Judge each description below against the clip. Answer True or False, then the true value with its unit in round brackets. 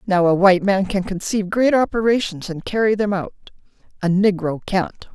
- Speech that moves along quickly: False (175 wpm)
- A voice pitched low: False (195 Hz)